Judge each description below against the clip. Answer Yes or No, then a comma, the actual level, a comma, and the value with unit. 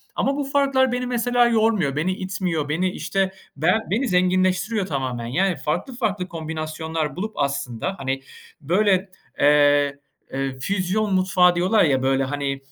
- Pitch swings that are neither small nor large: No, wide, 6.2 semitones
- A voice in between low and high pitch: Yes, medium, 180 Hz